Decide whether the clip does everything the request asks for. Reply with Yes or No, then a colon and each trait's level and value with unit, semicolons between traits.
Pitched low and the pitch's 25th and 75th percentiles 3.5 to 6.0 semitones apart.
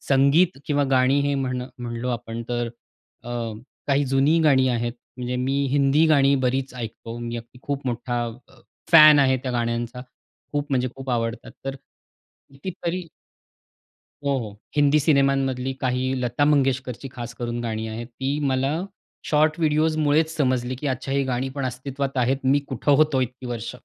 No: low, 130 Hz; average, 2.7 semitones